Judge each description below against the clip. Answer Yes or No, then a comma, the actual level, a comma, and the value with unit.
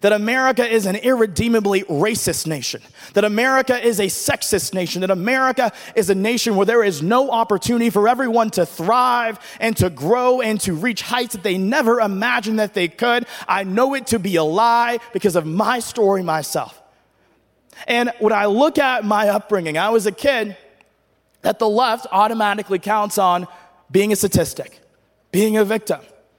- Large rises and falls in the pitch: No, average, 3.6 semitones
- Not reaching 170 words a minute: No, average, 175 wpm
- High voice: Yes, high, 215 Hz